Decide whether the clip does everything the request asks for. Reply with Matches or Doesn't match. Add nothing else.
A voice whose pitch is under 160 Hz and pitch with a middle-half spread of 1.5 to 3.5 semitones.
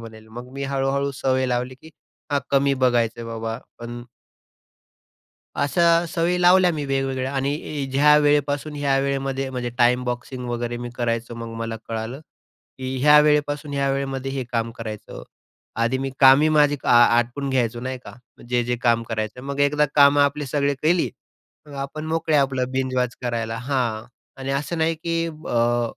Matches